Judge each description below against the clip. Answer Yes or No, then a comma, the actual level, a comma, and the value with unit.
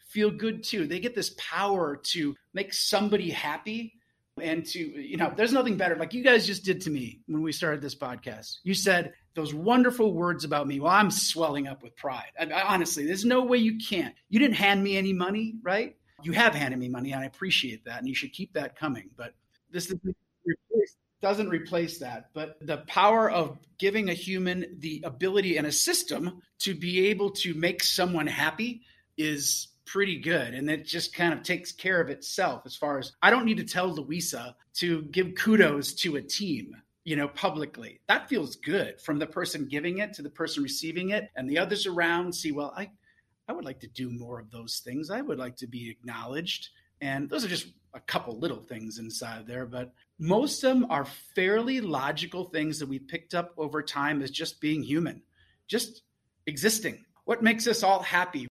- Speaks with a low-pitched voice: No, medium, 170 Hz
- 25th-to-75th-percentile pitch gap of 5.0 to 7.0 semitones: Yes, average, 5.3 semitones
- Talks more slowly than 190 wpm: No, fast, 205 wpm